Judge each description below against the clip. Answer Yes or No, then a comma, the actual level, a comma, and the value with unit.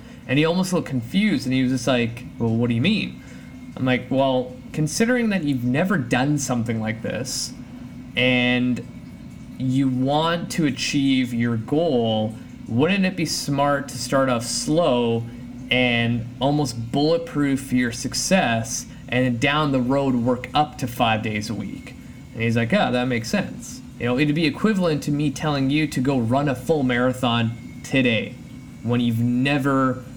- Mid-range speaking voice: No, low, 130 Hz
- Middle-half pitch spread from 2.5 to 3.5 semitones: Yes, average, 3.0 semitones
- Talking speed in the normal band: Yes, average, 165 wpm